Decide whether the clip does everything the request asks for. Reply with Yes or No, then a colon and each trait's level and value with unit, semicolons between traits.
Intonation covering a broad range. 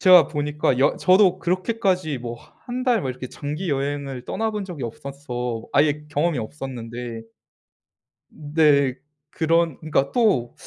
Yes: wide, 5.9 semitones